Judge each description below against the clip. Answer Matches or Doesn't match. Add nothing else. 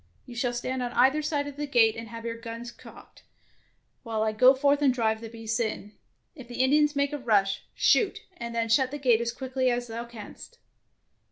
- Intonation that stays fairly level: Doesn't match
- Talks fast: Matches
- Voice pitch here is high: Matches